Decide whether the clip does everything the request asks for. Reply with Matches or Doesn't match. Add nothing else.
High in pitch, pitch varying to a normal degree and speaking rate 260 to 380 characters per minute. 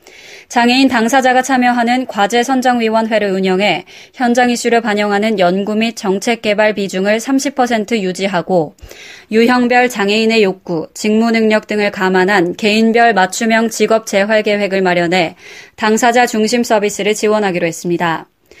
Matches